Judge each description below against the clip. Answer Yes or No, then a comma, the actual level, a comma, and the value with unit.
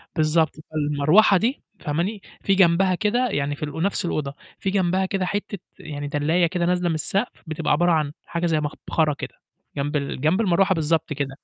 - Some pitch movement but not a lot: Yes, average, 4.1 semitones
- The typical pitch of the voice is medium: Yes, medium, 170 Hz